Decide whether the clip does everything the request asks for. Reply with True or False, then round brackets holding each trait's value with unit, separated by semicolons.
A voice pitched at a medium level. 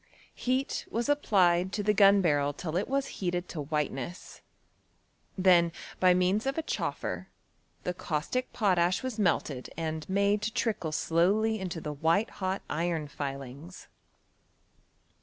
True (180 Hz)